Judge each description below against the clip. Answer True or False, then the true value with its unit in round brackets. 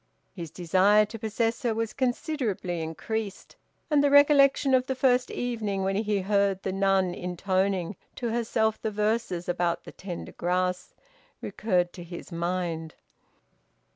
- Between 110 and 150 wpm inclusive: True (140 wpm)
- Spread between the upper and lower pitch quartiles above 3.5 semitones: True (4.1 semitones)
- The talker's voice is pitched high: True (200 Hz)